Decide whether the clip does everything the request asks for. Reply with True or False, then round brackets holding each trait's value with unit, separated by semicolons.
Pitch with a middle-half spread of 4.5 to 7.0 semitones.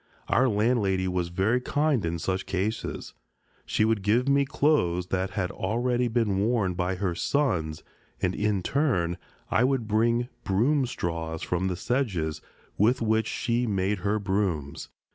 True (4.8 semitones)